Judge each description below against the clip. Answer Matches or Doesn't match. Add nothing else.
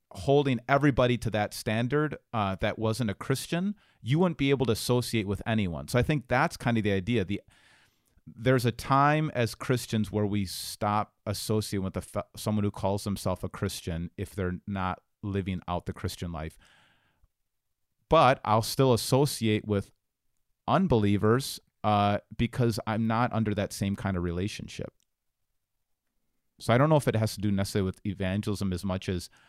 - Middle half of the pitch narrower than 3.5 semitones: Doesn't match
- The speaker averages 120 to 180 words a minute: Matches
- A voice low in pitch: Matches